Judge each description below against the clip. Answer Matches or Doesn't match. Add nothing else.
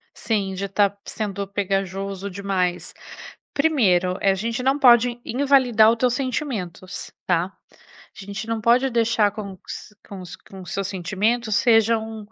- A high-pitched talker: Matches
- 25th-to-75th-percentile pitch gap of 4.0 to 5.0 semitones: Doesn't match